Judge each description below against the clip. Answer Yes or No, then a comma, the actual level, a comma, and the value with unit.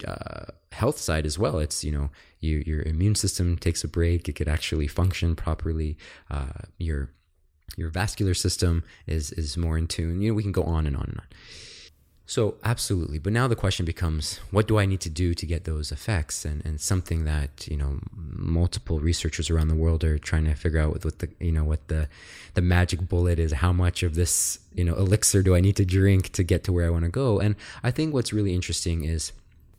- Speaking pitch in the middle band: No, very low, 85 Hz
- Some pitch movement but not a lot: Yes, average, 3.4 semitones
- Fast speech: Yes, fast, 225 wpm